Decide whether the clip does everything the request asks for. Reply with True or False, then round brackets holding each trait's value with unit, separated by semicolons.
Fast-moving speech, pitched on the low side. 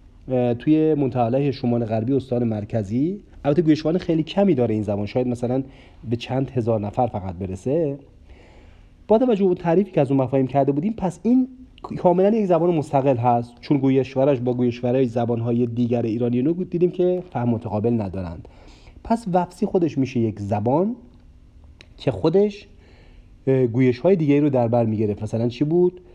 True (160 wpm; 130 Hz)